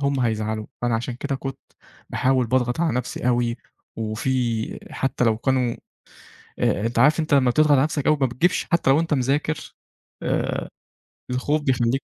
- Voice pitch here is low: Yes, low, 130 Hz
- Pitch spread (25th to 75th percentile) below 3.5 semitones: Yes, average, 3.1 semitones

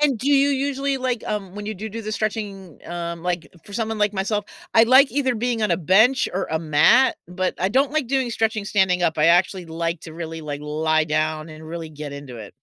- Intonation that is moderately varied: No, wide, 5.9 semitones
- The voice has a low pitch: No, high, 190 Hz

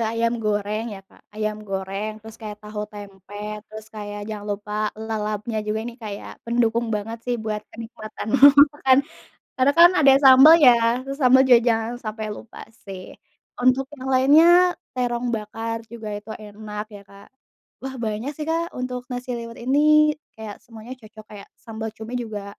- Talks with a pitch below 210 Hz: No, high, 225 Hz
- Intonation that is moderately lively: Yes, average, 3.1 semitones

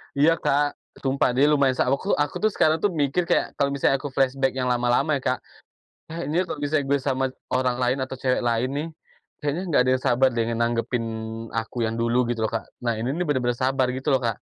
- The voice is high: No, low, 130 Hz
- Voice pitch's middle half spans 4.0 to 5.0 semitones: No, average, 3.0 semitones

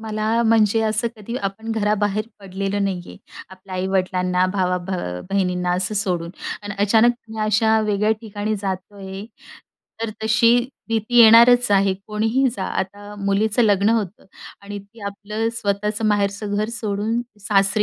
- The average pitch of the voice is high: Yes, high, 205 Hz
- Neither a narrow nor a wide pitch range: No, narrow, 2.0 semitones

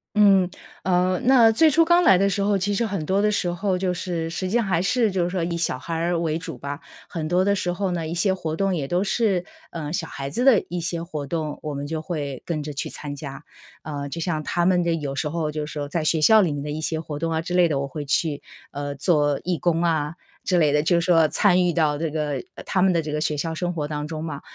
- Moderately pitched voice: Yes, medium, 165 Hz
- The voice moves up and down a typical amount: Yes, average, 3.4 semitones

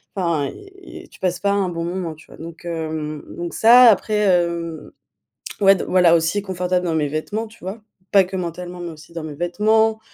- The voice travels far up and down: No, average, 3.3 semitones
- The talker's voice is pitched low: No, medium, 175 Hz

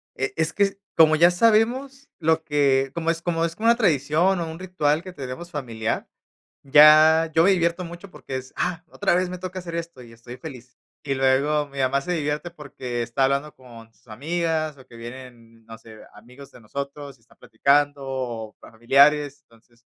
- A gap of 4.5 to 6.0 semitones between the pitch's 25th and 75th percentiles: Yes, average, 4.8 semitones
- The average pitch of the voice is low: No, medium, 145 Hz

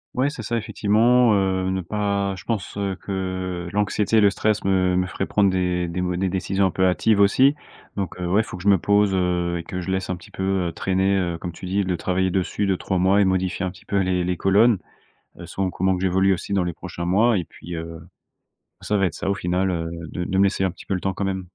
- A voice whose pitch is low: Yes, very low, 95 Hz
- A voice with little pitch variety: Yes, narrow, 1.7 semitones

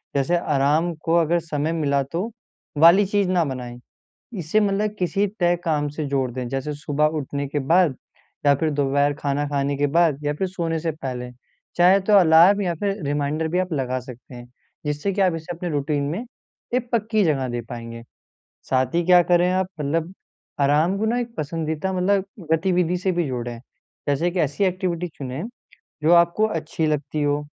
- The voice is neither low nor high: Yes, medium, 160 Hz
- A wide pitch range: No, average, 4.1 semitones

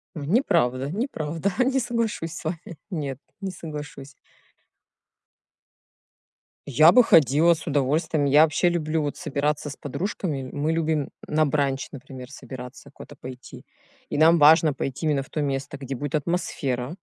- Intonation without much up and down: No, average, 3.2 semitones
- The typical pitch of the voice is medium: Yes, medium, 150 Hz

